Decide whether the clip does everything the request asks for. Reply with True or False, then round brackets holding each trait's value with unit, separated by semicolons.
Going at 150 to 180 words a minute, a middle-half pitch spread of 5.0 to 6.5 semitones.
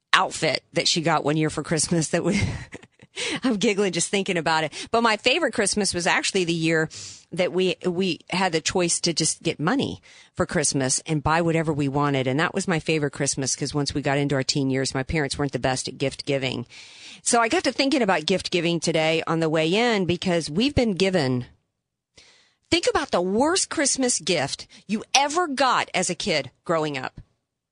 False (205 wpm; 5.3 semitones)